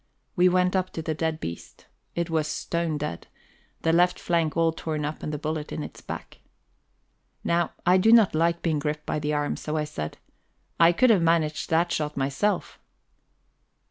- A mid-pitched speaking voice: Yes, medium, 160 Hz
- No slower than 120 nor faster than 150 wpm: No, average, 185 wpm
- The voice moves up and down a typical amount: No, narrow, 2.2 semitones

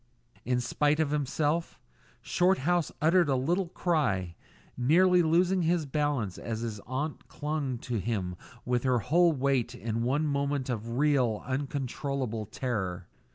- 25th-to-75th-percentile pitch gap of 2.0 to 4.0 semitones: No, average, 4.8 semitones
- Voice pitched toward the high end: No, medium, 140 Hz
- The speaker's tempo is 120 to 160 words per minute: Yes, slow, 135 wpm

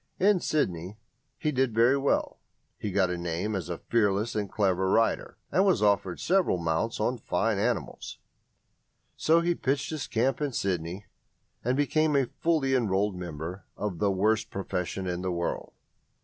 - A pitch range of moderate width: No, wide, 6.5 semitones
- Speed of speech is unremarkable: Yes, average, 165 wpm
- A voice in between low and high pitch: No, low, 105 Hz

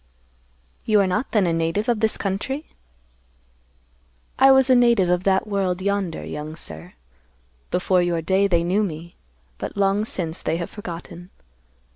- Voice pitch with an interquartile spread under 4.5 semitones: Yes, average, 3.4 semitones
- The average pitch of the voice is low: No, high, 190 Hz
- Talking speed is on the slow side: No, average, 155 wpm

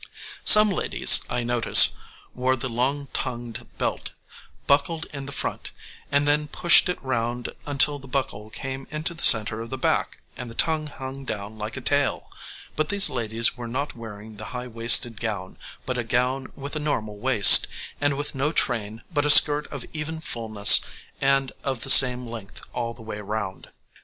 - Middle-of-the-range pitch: No, low, 125 Hz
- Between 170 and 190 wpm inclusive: Yes, average, 180 wpm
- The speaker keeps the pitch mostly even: No, average, 3.9 semitones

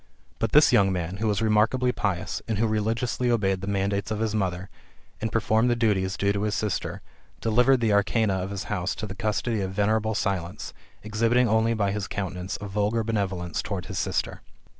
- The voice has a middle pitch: No, low, 105 Hz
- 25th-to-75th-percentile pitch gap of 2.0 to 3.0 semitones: Yes, narrow, 2.4 semitones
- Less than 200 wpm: No, fast, 205 wpm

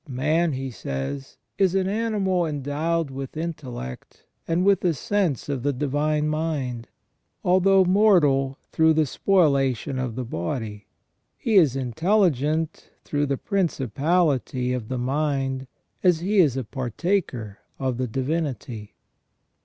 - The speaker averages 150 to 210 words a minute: No, slow, 135 wpm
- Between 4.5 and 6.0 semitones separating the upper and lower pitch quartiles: Yes, average, 5.0 semitones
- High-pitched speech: No, medium, 145 Hz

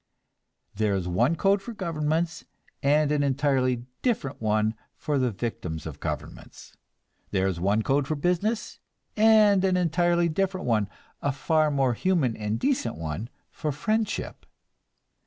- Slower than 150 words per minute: Yes, average, 140 wpm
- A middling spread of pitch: No, wide, 7.9 semitones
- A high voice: No, medium, 145 Hz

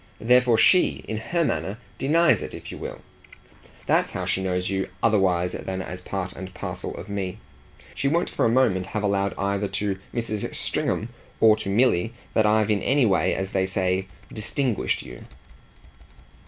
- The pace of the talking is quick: No, average, 170 wpm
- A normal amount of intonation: Yes, average, 3.3 semitones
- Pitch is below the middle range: Yes, low, 100 Hz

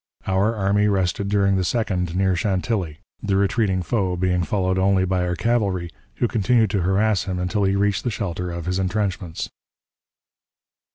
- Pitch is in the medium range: No, very low, 95 Hz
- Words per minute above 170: No, average, 165 wpm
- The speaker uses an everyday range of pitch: No, narrow, 2.2 semitones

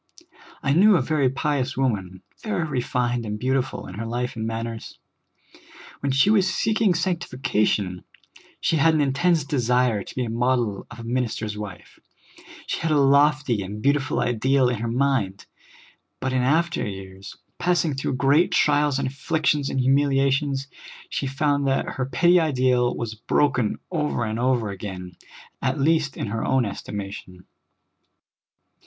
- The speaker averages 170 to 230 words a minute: No, average, 155 wpm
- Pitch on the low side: Yes, low, 130 Hz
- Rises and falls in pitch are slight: No, average, 4.2 semitones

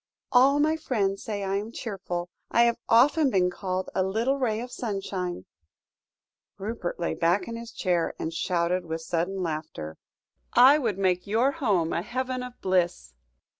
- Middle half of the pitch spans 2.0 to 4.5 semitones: No, average, 5.2 semitones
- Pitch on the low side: No, high, 195 Hz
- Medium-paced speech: Yes, average, 165 wpm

